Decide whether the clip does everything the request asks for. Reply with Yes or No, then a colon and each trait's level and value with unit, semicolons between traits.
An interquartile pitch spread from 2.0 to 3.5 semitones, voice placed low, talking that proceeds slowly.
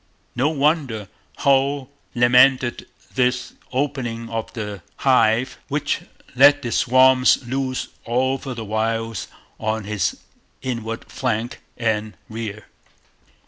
Yes: average, 2.8 semitones; low, 120 Hz; slow, 105 wpm